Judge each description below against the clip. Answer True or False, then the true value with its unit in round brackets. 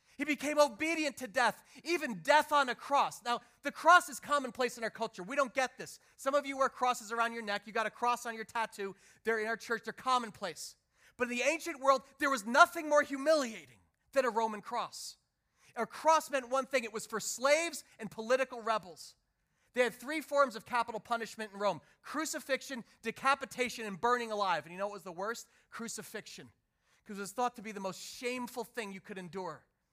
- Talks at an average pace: False (210 wpm)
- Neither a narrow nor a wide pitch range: True (4.2 semitones)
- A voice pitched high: True (240 Hz)